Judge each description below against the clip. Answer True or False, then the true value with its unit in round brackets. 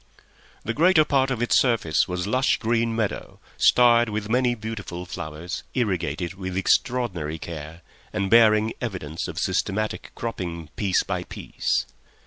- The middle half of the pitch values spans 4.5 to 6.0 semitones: True (5.2 semitones)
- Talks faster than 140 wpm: False (135 wpm)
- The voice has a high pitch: False (105 Hz)